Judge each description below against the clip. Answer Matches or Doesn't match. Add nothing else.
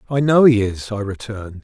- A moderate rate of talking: Doesn't match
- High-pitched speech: Doesn't match